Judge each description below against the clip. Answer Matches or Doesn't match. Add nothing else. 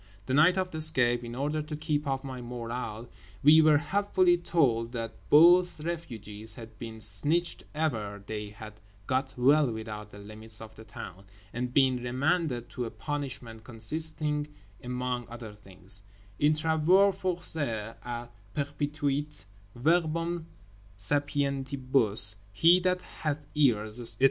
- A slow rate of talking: Matches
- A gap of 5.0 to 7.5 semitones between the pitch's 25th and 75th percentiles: Matches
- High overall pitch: Doesn't match